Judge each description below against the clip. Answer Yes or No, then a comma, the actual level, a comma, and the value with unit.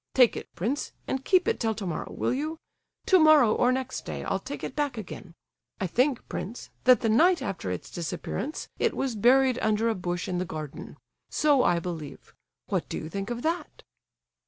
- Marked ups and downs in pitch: Yes, wide, 7.1 semitones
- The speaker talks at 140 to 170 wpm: No, average, 185 wpm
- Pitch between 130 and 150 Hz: No, high, 235 Hz